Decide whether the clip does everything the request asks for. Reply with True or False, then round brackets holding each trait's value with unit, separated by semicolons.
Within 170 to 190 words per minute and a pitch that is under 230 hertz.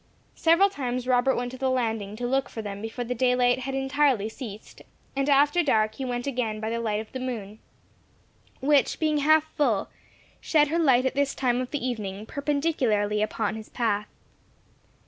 False (185 wpm; 250 Hz)